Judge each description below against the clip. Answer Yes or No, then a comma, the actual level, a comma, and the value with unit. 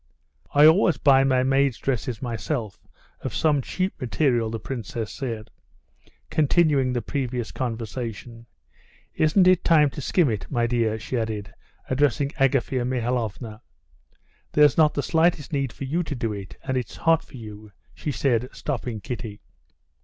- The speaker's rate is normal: Yes, average, 150 wpm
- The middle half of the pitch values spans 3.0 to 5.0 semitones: Yes, average, 4.0 semitones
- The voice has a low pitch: Yes, low, 130 Hz